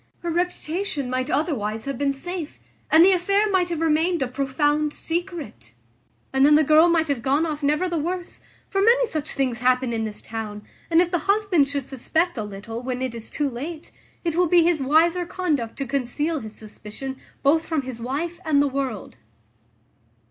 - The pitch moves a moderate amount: Yes, average, 5.0 semitones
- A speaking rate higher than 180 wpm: Yes, average, 190 wpm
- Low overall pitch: No, very high, 295 Hz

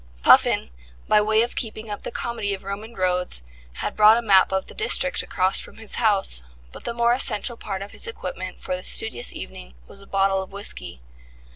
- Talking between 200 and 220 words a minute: Yes, fast, 205 wpm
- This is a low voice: No, high, 205 Hz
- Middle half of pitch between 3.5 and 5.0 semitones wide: No, average, 2.8 semitones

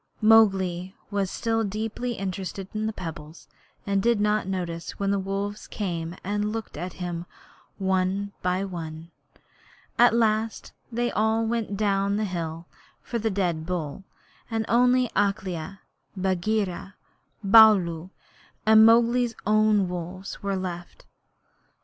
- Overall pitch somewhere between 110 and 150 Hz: No, high, 195 Hz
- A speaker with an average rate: No, slow, 130 wpm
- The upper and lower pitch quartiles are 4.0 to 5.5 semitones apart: No, average, 3.2 semitones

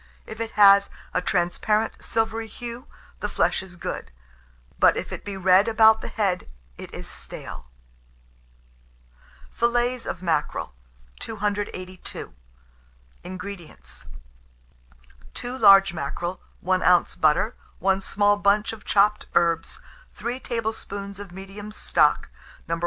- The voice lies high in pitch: Yes, high, 200 Hz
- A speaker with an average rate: No, slow, 120 wpm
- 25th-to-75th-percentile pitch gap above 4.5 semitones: No, average, 3.3 semitones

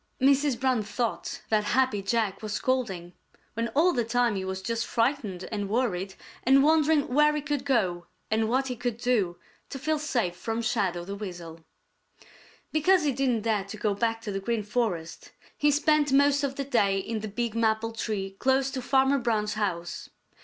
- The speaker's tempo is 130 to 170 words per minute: No, average, 185 wpm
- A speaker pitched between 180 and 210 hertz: No, high, 230 Hz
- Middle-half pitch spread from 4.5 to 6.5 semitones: Yes, average, 4.8 semitones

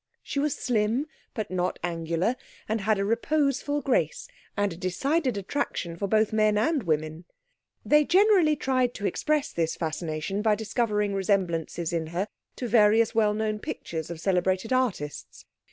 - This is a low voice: No, high, 210 Hz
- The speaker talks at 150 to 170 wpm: Yes, average, 155 wpm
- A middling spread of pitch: No, wide, 6.0 semitones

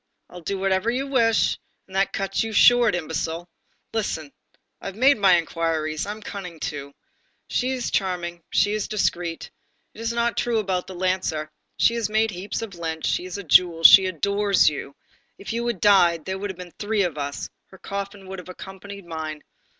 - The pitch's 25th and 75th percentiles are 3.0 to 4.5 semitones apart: Yes, average, 3.7 semitones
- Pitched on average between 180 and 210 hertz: Yes, high, 190 Hz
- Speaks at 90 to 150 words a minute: No, average, 190 wpm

